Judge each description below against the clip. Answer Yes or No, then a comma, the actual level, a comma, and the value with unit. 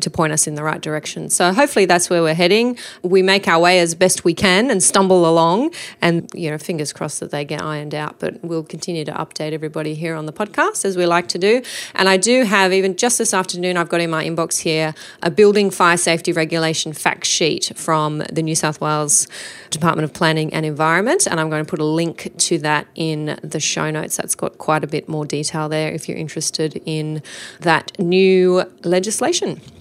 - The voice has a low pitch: No, medium, 165 Hz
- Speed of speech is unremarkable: No, fast, 215 wpm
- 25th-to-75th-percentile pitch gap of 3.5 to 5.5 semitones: No, average, 3.1 semitones